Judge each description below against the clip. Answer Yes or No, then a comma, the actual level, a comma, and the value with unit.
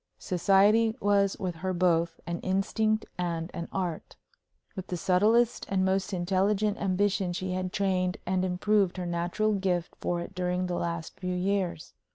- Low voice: No, medium, 185 Hz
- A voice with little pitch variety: Yes, narrow, 2.0 semitones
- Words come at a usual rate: Yes, average, 160 wpm